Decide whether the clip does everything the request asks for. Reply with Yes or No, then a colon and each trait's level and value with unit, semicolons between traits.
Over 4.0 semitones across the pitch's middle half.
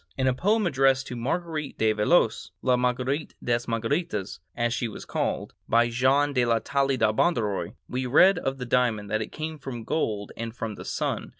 No: average, 3.3 semitones